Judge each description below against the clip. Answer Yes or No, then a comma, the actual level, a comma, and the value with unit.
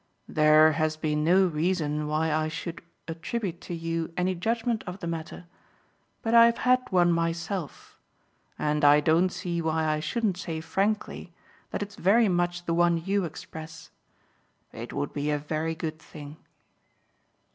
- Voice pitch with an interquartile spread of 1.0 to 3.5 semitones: Yes, average, 2.9 semitones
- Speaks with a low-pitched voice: No, medium, 165 Hz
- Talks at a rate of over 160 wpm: No, average, 155 wpm